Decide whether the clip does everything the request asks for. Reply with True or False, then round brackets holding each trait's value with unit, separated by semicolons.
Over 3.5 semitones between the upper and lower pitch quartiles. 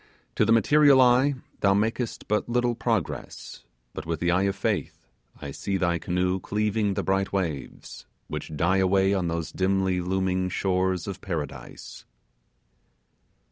False (2.7 semitones)